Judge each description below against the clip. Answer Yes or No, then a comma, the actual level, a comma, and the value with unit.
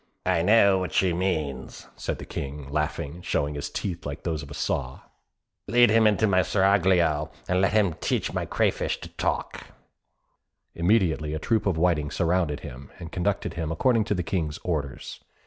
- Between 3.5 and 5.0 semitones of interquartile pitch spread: Yes, average, 4.3 semitones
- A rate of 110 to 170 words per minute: No, average, 180 wpm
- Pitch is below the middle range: Yes, very low, 85 Hz